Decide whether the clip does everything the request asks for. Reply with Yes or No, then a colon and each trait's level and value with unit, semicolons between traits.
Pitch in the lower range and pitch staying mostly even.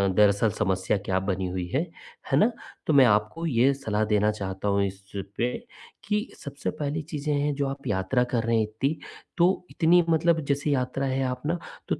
No: low, 130 Hz; wide, 6.1 semitones